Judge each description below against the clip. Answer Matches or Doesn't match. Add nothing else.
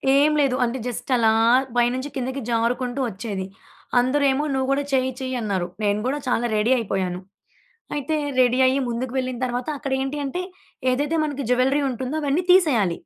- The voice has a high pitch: Matches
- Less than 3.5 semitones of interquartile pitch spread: Matches